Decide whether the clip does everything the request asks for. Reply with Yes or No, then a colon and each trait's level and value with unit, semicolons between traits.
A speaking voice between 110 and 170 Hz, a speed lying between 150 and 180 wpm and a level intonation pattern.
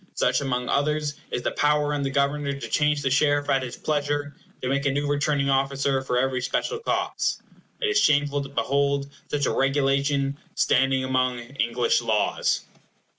Yes: medium, 140 Hz; average, 175 wpm; narrow, 1.5 semitones